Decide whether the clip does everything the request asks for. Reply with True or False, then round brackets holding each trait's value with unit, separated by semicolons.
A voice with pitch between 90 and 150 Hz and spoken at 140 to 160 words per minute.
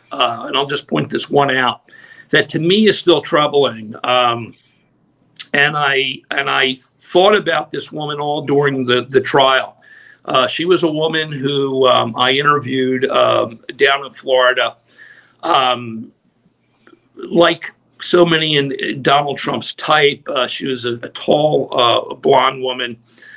True (135 Hz; 150 wpm)